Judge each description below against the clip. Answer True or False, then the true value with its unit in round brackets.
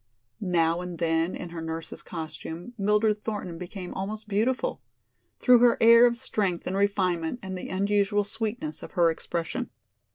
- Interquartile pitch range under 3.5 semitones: False (4.3 semitones)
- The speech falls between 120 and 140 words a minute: False (155 wpm)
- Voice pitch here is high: True (195 Hz)